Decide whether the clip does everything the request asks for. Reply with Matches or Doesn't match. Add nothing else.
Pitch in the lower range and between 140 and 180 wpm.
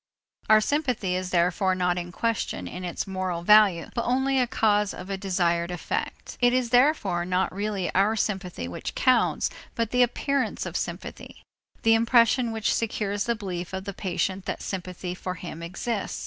Doesn't match